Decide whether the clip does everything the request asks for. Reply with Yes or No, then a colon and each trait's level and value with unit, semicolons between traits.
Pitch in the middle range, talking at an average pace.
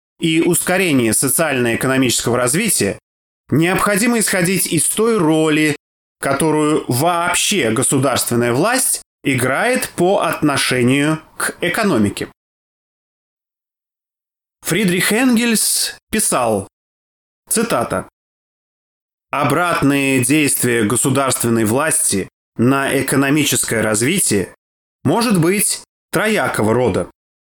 No: medium, 145 Hz; slow, 70 wpm